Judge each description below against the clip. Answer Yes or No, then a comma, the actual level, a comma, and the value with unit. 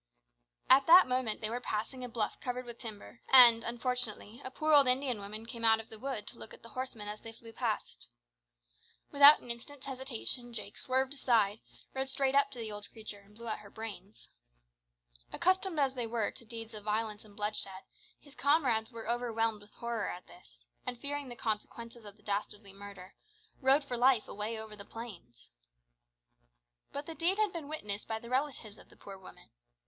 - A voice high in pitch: Yes, high, 230 Hz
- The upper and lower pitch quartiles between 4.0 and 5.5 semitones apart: No, average, 3.6 semitones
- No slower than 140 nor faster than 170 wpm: No, average, 195 wpm